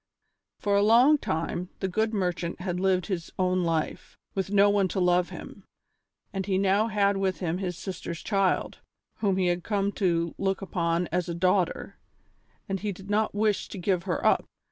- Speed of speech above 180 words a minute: Yes, average, 190 wpm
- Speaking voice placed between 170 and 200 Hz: Yes, high, 190 Hz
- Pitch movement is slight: Yes, narrow, 2.1 semitones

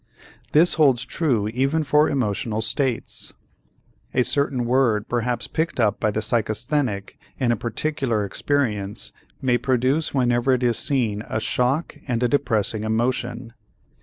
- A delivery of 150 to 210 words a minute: No, slow, 135 wpm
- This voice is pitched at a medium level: No, low, 120 Hz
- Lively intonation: No, average, 3.5 semitones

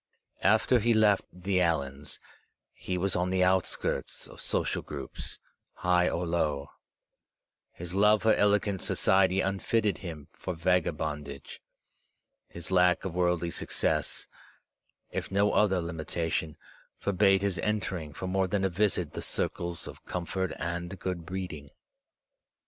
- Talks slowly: Yes, slow, 130 wpm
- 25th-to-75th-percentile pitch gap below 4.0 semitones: Yes, narrow, 2.4 semitones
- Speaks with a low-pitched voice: Yes, very low, 90 Hz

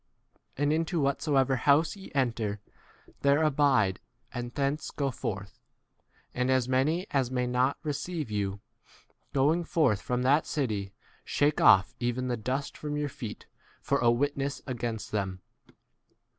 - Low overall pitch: Yes, low, 130 Hz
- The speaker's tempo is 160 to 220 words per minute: No, average, 145 wpm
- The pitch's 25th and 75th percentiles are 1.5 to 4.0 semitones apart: Yes, average, 3.6 semitones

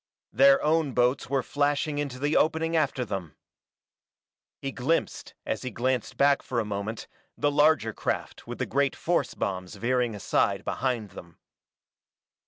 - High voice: No, low, 130 Hz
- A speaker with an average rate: Yes, average, 150 wpm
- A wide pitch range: No, average, 4.4 semitones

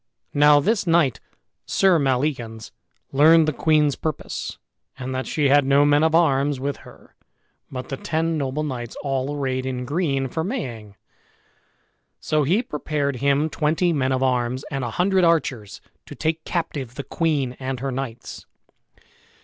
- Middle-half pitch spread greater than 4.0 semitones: No, average, 3.3 semitones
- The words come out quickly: No, average, 155 wpm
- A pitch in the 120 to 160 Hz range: Yes, medium, 140 Hz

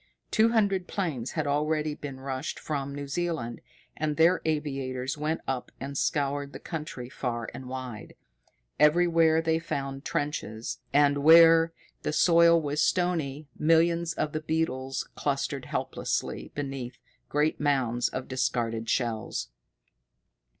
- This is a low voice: No, medium, 145 Hz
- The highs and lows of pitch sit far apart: No, average, 3.5 semitones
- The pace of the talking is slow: Yes, slow, 130 wpm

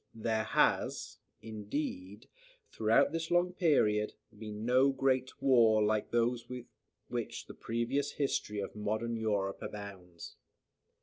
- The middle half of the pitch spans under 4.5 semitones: Yes, average, 3.6 semitones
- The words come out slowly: Yes, slow, 120 wpm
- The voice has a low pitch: Yes, low, 115 Hz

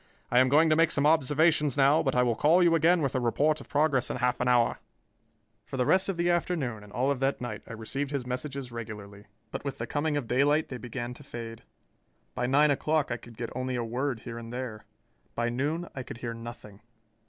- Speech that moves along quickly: Yes, fast, 235 wpm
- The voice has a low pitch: Yes, low, 130 Hz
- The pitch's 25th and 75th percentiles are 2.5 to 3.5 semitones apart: No, average, 3.9 semitones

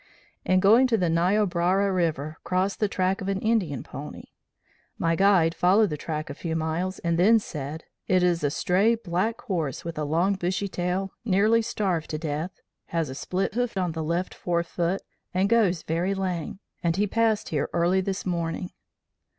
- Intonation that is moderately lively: Yes, average, 3.0 semitones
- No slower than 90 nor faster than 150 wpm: No, average, 185 wpm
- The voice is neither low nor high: Yes, medium, 180 Hz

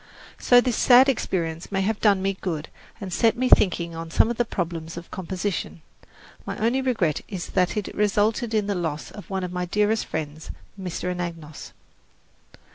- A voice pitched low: No, high, 190 Hz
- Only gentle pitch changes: No, average, 4.3 semitones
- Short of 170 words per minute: No, average, 180 wpm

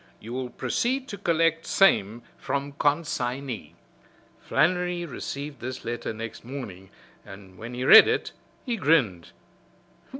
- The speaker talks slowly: Yes, slow, 125 wpm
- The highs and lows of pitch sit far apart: Yes, wide, 6.3 semitones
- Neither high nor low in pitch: No, low, 130 Hz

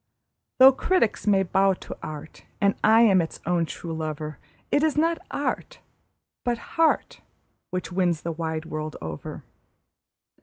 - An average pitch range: No, wide, 6.5 semitones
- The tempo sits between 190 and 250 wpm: No, average, 145 wpm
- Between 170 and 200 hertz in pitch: Yes, medium, 185 Hz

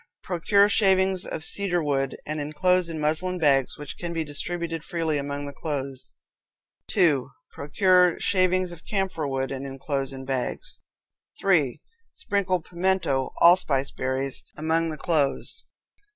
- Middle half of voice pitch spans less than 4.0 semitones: No, average, 4.6 semitones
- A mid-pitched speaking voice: Yes, medium, 160 Hz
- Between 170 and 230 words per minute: No, slow, 135 wpm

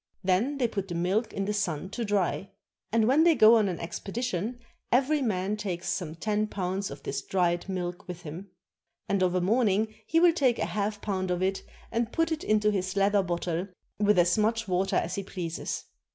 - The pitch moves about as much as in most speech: Yes, average, 3.5 semitones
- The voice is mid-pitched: No, high, 200 Hz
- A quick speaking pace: Yes, fast, 210 wpm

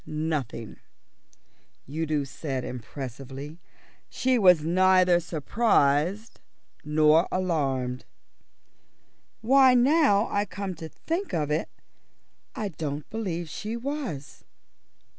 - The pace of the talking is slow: Yes, slow, 90 wpm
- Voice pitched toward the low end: No, medium, 165 Hz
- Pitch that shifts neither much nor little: No, wide, 6.2 semitones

